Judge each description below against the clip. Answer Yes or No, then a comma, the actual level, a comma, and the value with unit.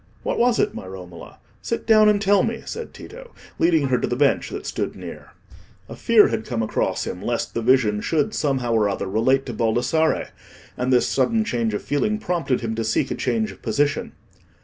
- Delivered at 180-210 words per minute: Yes, fast, 205 wpm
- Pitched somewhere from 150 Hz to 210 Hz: No, low, 135 Hz